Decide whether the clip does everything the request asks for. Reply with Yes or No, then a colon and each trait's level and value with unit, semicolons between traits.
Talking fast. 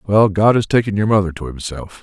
Yes: fast, 235 wpm